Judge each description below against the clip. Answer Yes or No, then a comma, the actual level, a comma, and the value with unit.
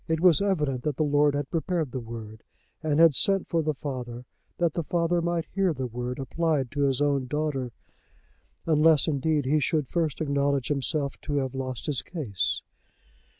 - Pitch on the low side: No, medium, 145 Hz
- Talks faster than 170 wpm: Yes, average, 180 wpm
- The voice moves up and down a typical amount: Yes, average, 3.5 semitones